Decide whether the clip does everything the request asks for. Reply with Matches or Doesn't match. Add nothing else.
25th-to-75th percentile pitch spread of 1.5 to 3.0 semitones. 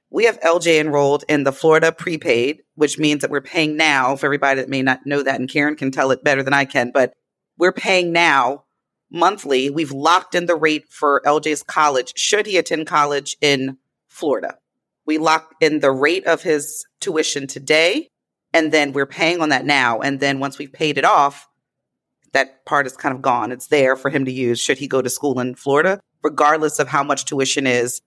Matches